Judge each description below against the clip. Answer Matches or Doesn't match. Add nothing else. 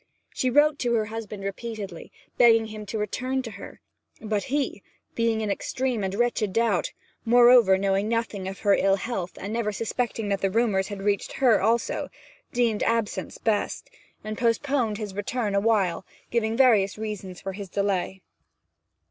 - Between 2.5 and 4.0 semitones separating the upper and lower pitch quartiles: Matches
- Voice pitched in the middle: Doesn't match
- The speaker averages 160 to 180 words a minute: Matches